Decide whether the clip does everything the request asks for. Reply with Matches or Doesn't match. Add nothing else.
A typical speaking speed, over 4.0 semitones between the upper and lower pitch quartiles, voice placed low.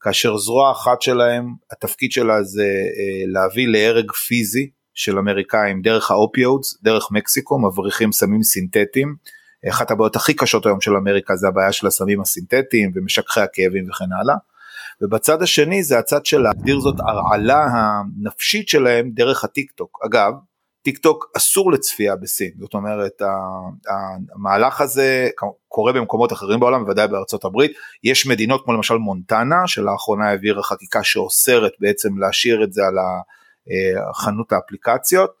Matches